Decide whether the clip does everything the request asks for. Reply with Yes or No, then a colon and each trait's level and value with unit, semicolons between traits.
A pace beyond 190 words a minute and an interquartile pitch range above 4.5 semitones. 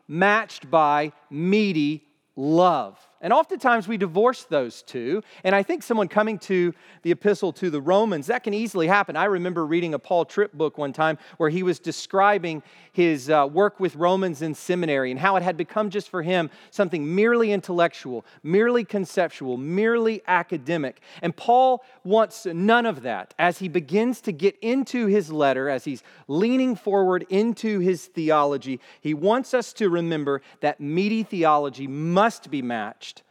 No: average, 165 wpm; average, 4.9 semitones